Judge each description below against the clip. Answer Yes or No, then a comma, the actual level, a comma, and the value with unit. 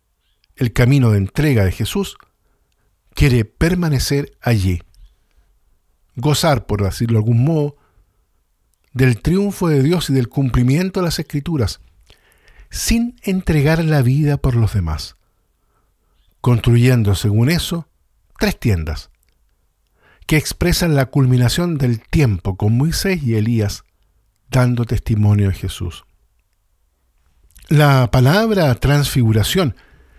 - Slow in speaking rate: Yes, slow, 105 wpm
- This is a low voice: Yes, low, 120 Hz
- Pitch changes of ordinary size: No, wide, 7.4 semitones